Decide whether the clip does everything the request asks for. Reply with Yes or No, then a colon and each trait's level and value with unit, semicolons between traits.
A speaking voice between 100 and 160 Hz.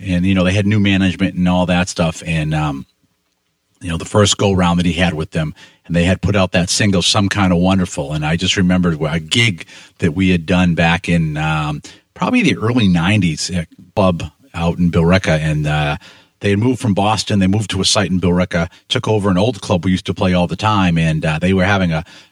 No: very low, 90 Hz